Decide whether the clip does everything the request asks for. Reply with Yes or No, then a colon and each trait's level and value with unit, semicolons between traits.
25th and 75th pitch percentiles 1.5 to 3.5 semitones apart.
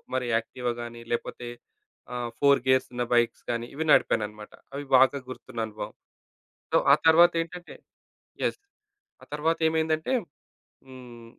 No: average, 5.1 semitones